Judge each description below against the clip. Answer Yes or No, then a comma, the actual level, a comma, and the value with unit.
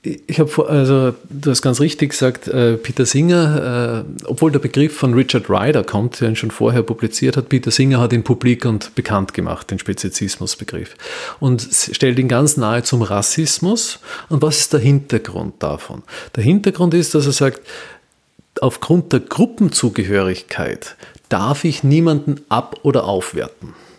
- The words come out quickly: No, average, 155 wpm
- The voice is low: Yes, low, 130 Hz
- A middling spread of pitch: Yes, average, 4.5 semitones